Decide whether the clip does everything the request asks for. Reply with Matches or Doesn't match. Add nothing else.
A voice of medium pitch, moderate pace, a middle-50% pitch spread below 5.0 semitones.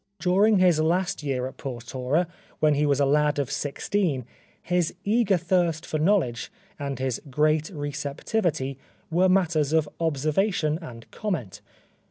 Matches